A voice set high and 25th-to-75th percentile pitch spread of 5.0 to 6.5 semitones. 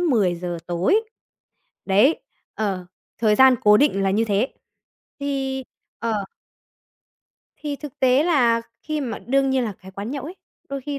Yes: high, 245 Hz; wide, 5.4 semitones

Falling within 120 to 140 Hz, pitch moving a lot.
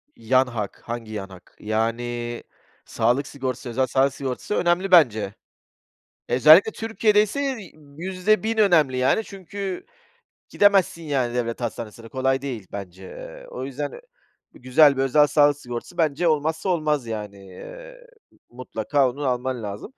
Yes: low, 135 Hz; wide, 6.0 semitones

